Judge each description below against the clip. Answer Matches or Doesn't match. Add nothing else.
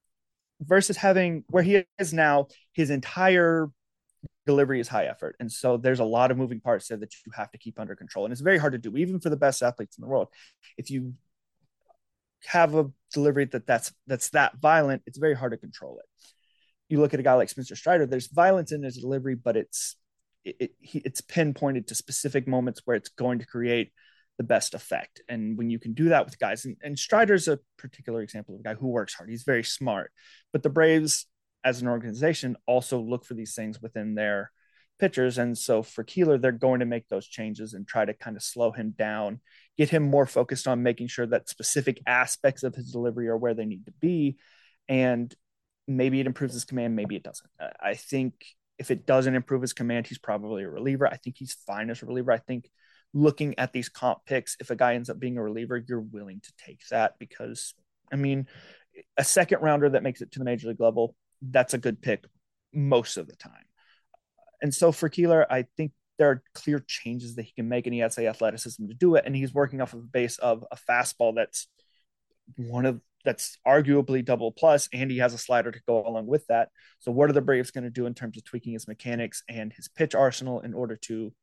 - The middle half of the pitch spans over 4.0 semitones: Doesn't match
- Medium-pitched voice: Doesn't match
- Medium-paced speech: Doesn't match